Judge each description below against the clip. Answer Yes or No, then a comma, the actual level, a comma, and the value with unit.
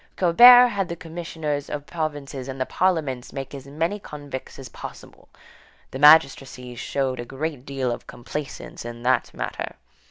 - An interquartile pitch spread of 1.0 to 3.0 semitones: No, average, 3.7 semitones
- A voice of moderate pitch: Yes, medium, 145 Hz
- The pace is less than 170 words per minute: Yes, average, 155 wpm